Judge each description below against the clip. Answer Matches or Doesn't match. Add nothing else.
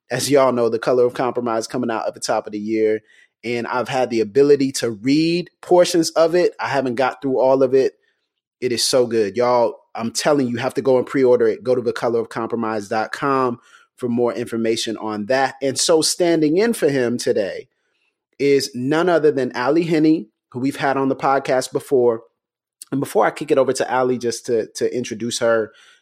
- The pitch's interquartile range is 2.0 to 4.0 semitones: Doesn't match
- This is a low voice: Matches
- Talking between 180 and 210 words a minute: Matches